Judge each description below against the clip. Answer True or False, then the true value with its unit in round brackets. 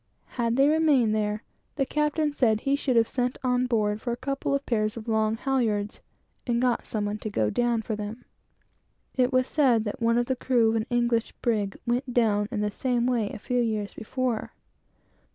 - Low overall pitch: False (235 Hz)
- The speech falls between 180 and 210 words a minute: True (205 wpm)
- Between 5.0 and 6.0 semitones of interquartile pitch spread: False (2.8 semitones)